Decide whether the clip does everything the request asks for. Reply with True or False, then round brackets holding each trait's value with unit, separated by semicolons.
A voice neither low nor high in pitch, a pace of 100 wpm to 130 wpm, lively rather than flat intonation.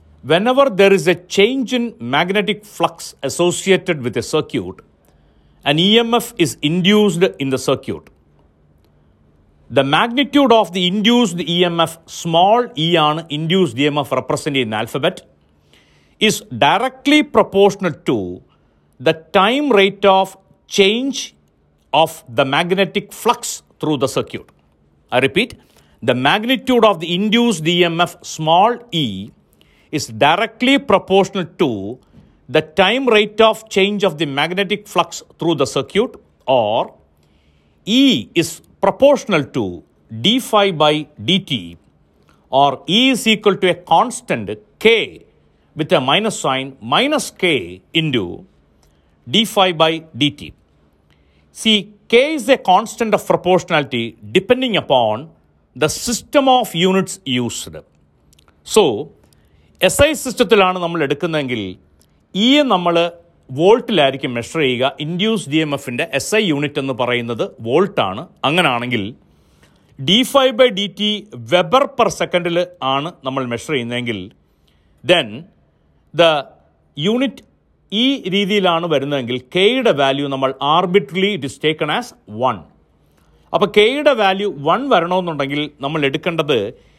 True (170 Hz; 120 wpm; 7.4 semitones)